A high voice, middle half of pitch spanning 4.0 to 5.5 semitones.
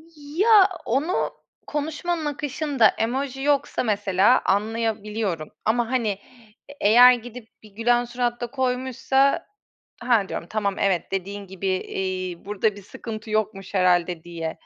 Yes: high, 225 Hz; average, 4.9 semitones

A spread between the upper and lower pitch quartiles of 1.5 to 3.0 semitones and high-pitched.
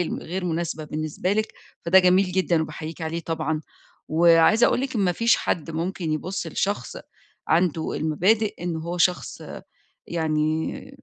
No: average, 2.7 semitones; medium, 170 Hz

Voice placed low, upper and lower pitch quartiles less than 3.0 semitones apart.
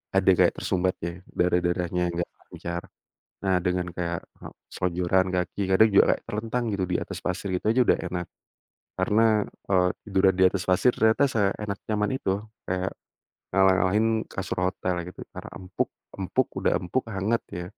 Yes: very low, 95 Hz; narrow, 2.4 semitones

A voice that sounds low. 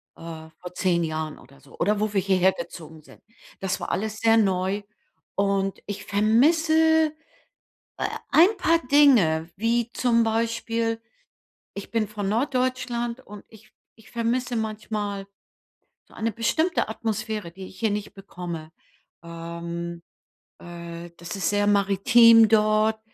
No: high, 210 Hz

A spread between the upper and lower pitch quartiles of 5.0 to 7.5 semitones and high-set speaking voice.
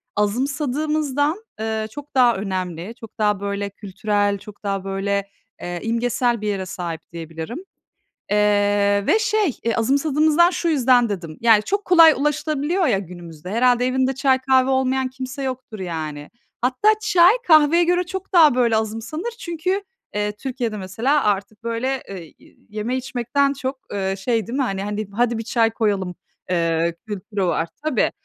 Yes: wide, 5.5 semitones; high, 230 Hz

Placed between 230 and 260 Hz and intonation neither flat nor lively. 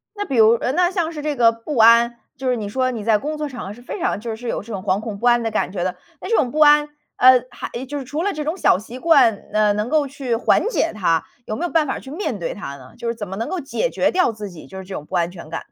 No: high, 240 Hz; wide, 6.2 semitones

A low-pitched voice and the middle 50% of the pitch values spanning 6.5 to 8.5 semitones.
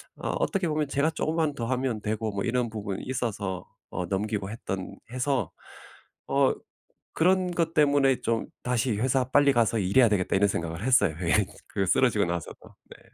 No: low, 120 Hz; wide, 5.6 semitones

